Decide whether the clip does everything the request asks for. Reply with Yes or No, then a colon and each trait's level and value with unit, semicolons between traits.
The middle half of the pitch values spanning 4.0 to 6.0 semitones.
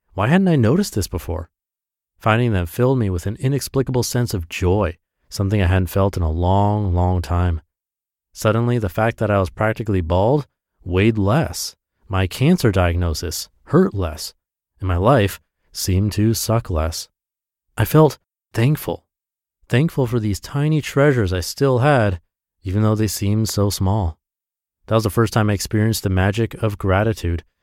Yes: average, 4.3 semitones